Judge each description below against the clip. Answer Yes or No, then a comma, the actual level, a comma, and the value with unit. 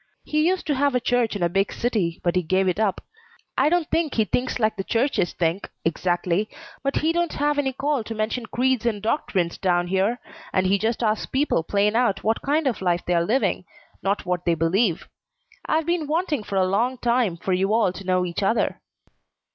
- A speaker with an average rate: No, fast, 210 wpm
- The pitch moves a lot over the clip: Yes, wide, 6.0 semitones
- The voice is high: Yes, high, 215 Hz